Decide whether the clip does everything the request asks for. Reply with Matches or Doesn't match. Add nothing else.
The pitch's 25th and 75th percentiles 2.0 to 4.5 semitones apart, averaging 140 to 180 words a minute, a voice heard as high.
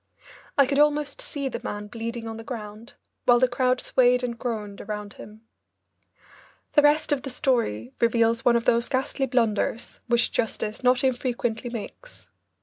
Matches